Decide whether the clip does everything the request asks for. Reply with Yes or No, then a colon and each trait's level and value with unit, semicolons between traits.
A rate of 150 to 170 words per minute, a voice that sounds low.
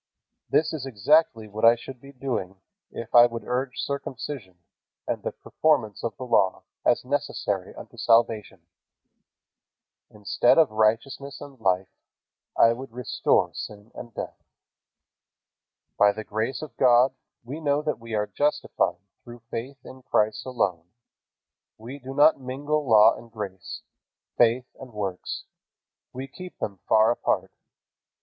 No: average, 140 wpm; low, 120 Hz